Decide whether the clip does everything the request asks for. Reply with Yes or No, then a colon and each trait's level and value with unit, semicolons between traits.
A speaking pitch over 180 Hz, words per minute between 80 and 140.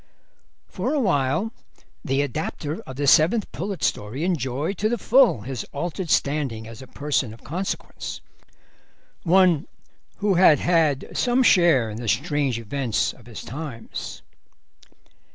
No: medium, 145 Hz; slow, 135 wpm